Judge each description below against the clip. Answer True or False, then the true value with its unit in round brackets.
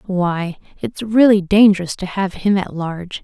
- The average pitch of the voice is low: False (190 Hz)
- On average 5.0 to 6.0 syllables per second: False (4.6 syllables/s)